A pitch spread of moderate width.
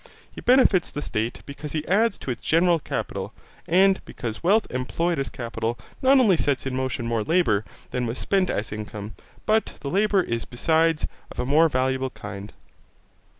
No: wide, 7.2 semitones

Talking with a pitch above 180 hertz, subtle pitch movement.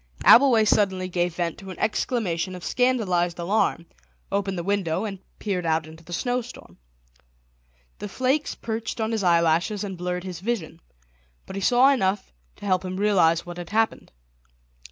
No: high, 190 Hz; average, 4.0 semitones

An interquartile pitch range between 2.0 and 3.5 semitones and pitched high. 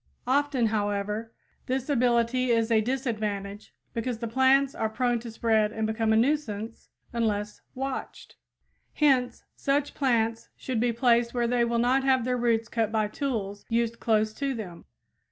Yes: narrow, 2.6 semitones; high, 235 Hz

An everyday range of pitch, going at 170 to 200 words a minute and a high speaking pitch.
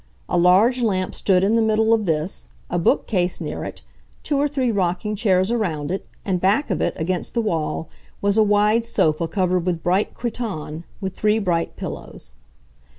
Yes: average, 3.8 semitones; average, 180 wpm; high, 195 Hz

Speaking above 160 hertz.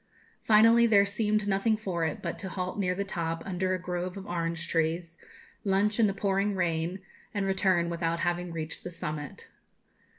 Yes: medium, 185 Hz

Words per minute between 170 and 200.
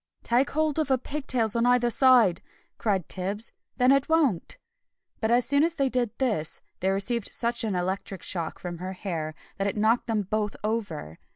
Yes: average, 190 wpm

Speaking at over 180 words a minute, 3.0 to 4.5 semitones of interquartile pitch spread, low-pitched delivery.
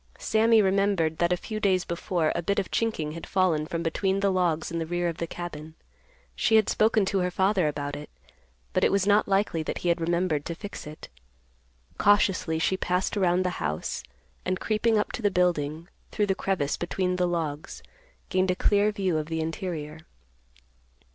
No: average, 195 wpm; average, 3.4 semitones; medium, 180 Hz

